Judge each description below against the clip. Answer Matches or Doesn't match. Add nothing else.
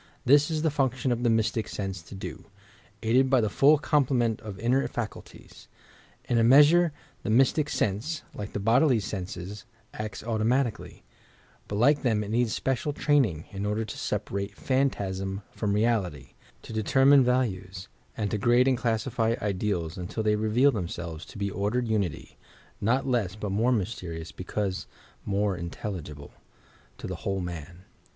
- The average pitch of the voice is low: Matches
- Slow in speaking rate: Doesn't match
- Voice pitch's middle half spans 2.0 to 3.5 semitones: Doesn't match